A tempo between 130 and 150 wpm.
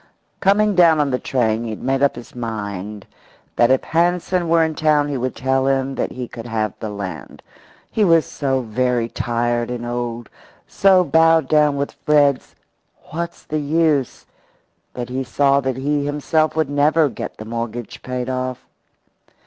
No: average, 170 wpm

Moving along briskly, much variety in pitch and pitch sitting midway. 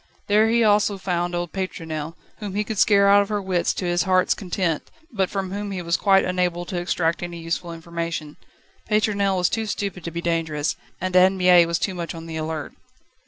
No: fast, 210 wpm; average, 2.8 semitones; medium, 180 Hz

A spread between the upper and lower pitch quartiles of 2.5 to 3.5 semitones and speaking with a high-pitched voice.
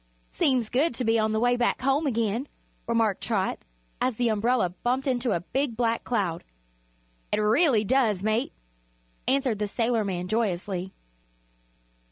Yes: average, 3.2 semitones; high, 230 Hz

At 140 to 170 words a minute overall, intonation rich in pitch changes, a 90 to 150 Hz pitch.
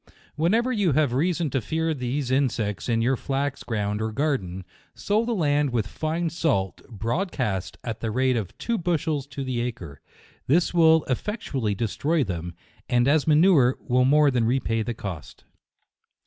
Yes: average, 165 wpm; wide, 5.7 semitones; low, 135 Hz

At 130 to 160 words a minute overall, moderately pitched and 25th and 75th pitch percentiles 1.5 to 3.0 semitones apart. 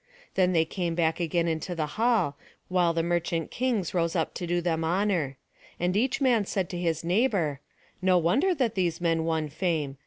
No: average, 190 wpm; medium, 175 Hz; average, 2.7 semitones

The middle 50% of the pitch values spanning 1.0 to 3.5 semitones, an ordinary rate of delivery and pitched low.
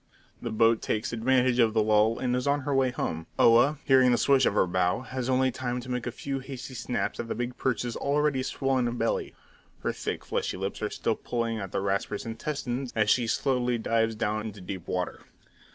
No: average, 2.9 semitones; fast, 210 wpm; low, 120 Hz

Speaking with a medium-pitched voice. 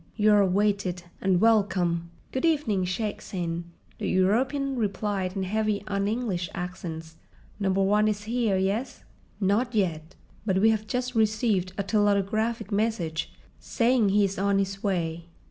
No: high, 200 Hz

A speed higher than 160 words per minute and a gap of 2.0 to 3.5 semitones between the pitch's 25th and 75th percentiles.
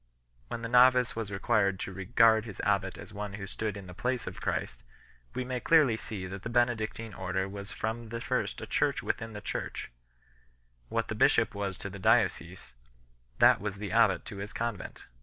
Yes: average, 195 wpm; average, 3.0 semitones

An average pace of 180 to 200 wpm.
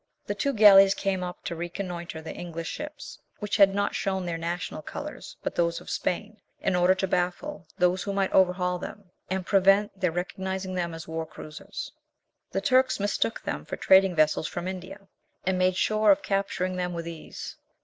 Yes: average, 185 wpm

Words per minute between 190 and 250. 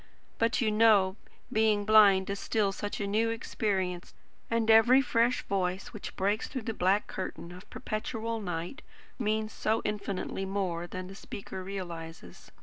No: average, 150 wpm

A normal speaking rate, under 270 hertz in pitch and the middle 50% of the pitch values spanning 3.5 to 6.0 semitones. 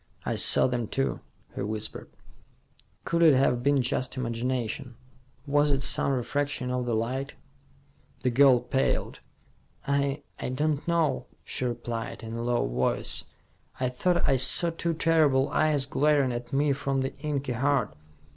No: average, 150 wpm; low, 135 Hz; average, 2.9 semitones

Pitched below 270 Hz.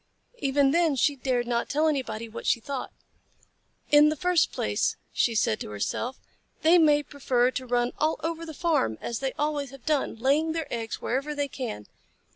No: very high, 275 Hz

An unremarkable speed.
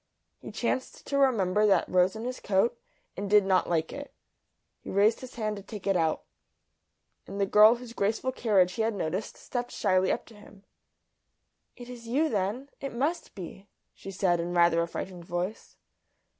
Yes: average, 185 wpm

